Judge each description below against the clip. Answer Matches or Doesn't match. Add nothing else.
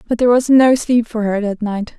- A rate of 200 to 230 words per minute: Doesn't match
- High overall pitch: Matches